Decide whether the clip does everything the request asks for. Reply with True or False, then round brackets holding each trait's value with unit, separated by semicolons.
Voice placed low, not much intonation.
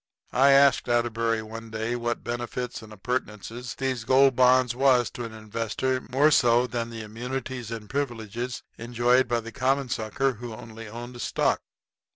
True (120 Hz; 2.0 semitones)